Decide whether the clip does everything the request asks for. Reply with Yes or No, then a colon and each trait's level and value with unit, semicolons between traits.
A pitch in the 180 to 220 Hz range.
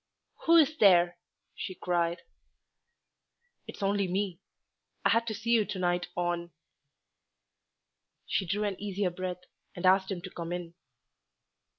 Yes: medium, 185 Hz